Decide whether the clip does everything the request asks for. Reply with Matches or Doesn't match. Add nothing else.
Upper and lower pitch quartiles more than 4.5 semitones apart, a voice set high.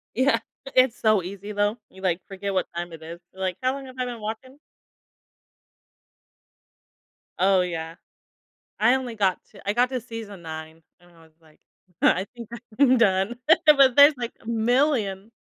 Matches